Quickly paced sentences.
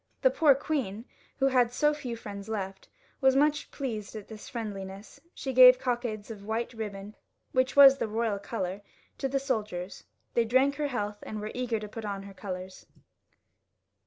No: average, 175 wpm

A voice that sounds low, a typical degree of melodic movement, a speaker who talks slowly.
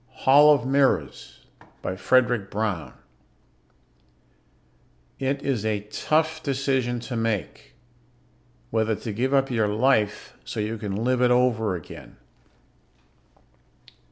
Yes: low, 120 Hz; average, 4.0 semitones; slow, 115 wpm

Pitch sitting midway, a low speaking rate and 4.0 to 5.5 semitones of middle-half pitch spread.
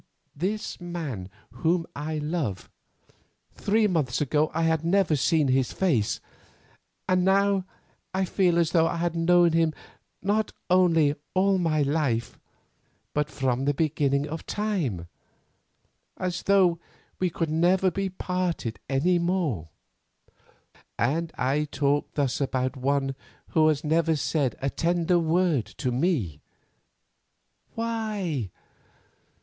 Yes: medium, 160 Hz; slow, 115 wpm; average, 4.4 semitones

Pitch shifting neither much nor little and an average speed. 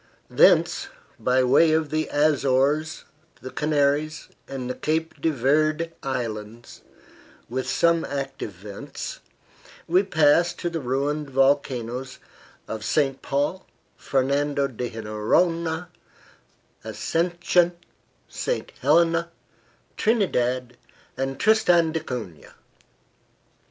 No: average, 4.1 semitones; slow, 95 wpm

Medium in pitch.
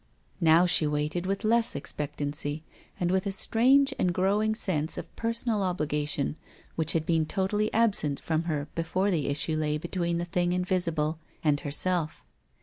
Yes: medium, 170 Hz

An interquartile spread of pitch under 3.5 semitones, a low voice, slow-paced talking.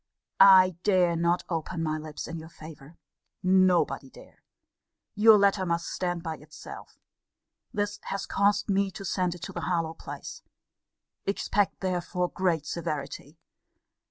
No: average, 2.9 semitones; medium, 180 Hz; slow, 130 wpm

